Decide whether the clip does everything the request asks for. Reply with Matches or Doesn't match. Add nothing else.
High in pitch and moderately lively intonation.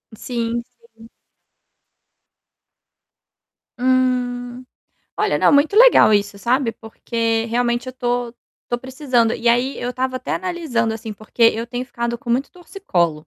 Doesn't match